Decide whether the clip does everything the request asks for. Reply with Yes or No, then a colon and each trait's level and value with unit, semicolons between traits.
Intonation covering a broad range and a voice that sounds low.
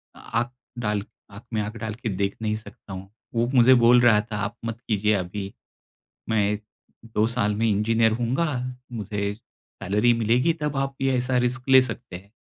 No: average, 2.7 semitones; low, 110 Hz